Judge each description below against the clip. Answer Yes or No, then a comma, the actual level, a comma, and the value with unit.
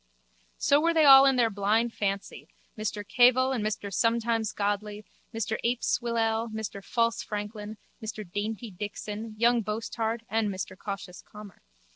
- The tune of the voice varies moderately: No, narrow, 2.1 semitones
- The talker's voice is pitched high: Yes, high, 220 Hz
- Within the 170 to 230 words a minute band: No, average, 145 wpm